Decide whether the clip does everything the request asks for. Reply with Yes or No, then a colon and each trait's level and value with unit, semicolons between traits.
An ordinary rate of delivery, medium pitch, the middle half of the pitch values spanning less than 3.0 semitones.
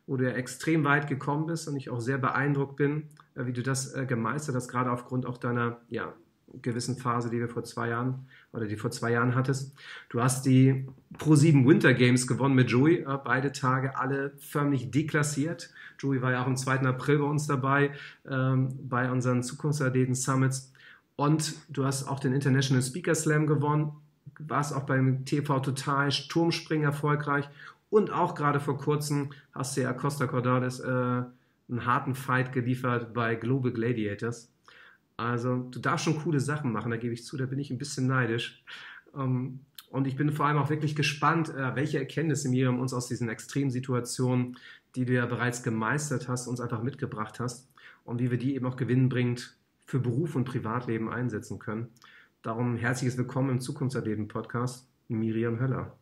No: average, 180 wpm; low, 130 Hz; narrow, 2.5 semitones